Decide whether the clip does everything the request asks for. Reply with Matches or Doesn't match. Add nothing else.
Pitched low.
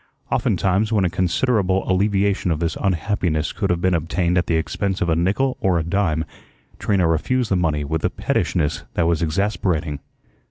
Matches